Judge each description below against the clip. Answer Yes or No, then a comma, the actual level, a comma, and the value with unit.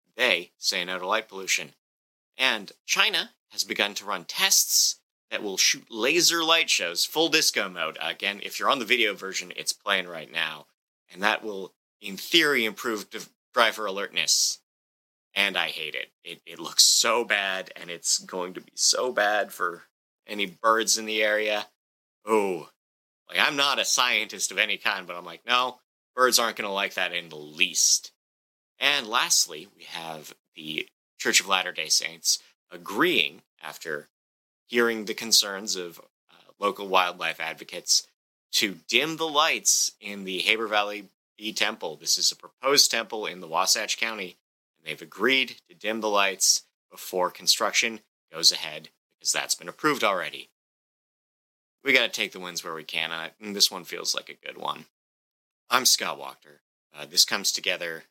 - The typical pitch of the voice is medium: No, low, 105 Hz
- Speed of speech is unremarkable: Yes, average, 170 wpm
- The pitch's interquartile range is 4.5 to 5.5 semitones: Yes, average, 5.1 semitones